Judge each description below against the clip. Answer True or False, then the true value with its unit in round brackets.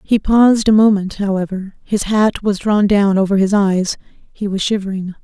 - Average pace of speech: True (185 wpm)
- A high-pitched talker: True (200 Hz)